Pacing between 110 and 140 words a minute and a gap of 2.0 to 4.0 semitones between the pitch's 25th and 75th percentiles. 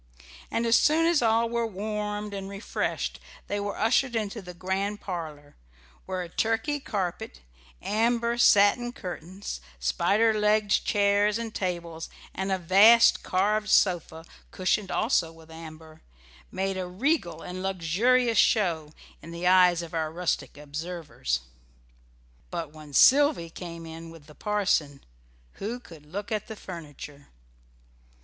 No: slow, 135 wpm; average, 4.7 semitones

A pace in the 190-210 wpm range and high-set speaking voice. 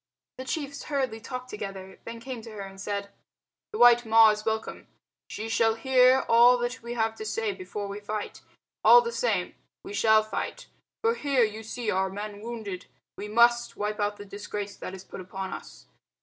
Yes: average, 195 wpm; high, 220 Hz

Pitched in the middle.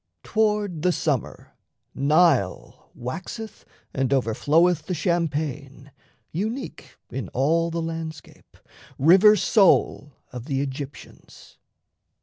Yes: medium, 160 Hz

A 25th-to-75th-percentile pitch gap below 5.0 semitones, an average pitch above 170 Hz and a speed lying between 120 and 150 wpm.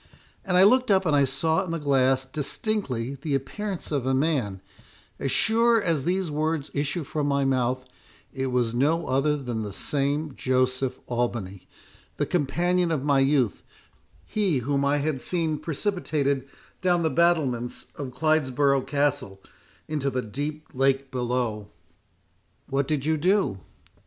No: average, 3.7 semitones; medium, 140 Hz; average, 140 wpm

